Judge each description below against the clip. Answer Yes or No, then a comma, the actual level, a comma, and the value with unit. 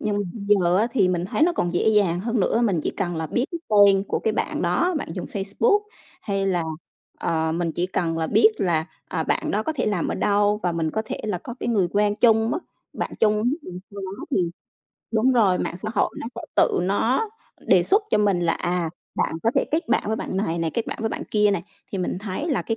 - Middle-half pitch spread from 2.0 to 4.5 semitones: Yes, average, 3.9 semitones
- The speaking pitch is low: No, high, 200 Hz